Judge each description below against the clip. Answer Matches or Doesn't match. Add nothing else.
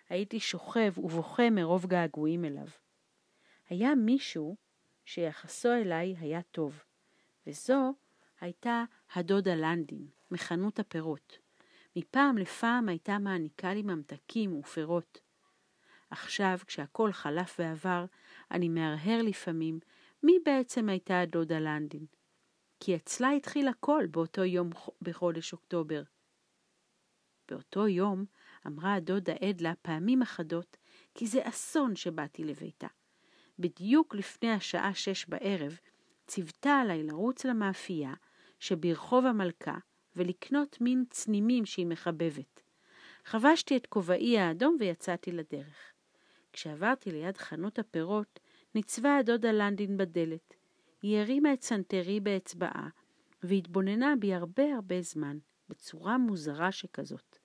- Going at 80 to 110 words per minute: Matches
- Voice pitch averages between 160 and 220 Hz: Matches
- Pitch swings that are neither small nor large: Matches